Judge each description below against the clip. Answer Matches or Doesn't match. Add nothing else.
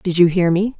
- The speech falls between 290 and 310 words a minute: Matches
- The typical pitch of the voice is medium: Matches